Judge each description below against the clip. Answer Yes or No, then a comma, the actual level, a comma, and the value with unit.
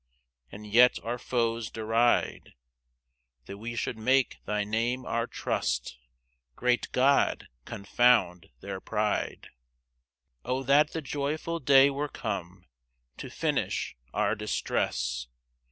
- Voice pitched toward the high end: No, low, 115 Hz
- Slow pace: Yes, slow, 115 wpm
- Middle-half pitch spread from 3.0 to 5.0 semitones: Yes, average, 3.9 semitones